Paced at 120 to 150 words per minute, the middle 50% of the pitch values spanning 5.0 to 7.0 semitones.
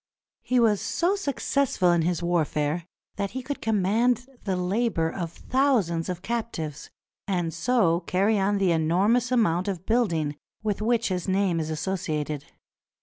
Yes: average, 145 wpm; wide, 5.6 semitones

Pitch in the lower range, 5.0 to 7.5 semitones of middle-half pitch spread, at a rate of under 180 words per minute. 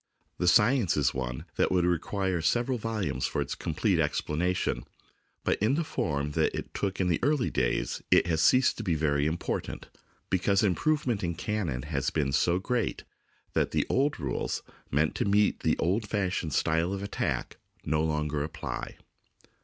Yes: very low, 90 Hz; wide, 5.6 semitones; average, 170 wpm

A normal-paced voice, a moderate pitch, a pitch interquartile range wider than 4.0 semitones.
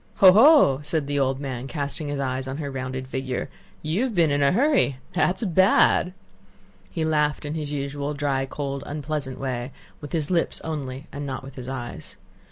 No: average, 180 wpm; medium, 145 Hz; average, 2.9 semitones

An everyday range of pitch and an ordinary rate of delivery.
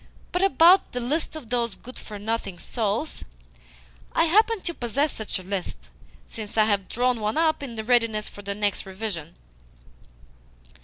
No: wide, 6.0 semitones; average, 160 wpm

